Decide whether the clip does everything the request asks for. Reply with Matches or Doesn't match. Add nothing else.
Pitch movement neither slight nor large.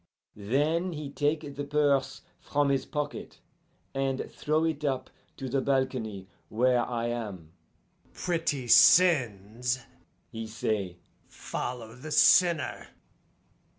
Matches